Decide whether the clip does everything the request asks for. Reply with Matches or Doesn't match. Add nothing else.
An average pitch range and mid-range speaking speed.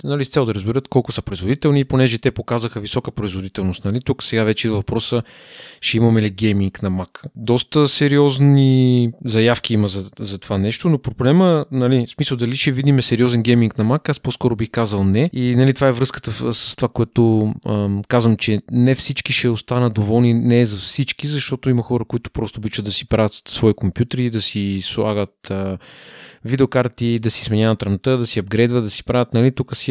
Doesn't match